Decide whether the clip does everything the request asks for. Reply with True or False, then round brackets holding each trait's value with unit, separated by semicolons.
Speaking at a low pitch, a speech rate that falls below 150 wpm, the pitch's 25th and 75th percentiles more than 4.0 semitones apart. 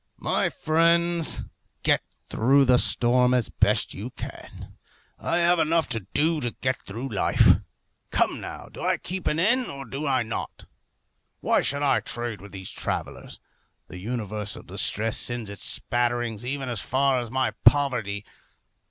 False (125 Hz; 155 wpm; 4.4 semitones)